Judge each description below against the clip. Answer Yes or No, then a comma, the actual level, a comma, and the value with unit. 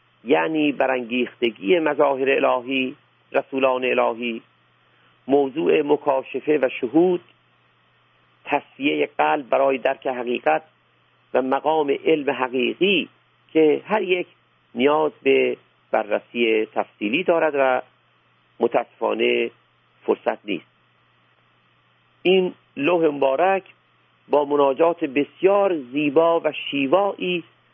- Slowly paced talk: Yes, slow, 85 wpm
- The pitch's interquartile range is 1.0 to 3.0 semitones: No, average, 4.5 semitones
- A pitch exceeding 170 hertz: No, medium, 140 Hz